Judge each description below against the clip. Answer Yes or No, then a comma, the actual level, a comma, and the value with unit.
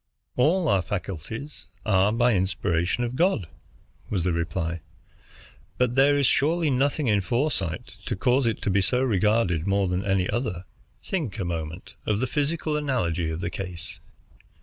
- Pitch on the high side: No, low, 105 Hz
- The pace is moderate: Yes, average, 160 wpm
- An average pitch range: No, wide, 6.4 semitones